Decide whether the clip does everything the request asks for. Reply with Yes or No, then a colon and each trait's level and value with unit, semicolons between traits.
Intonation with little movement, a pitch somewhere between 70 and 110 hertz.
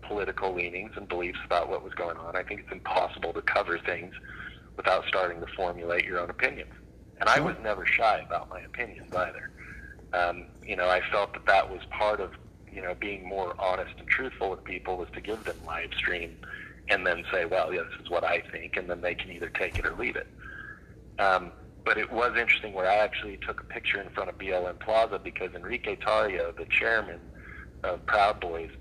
No: average, 3.2 semitones; very low, 90 Hz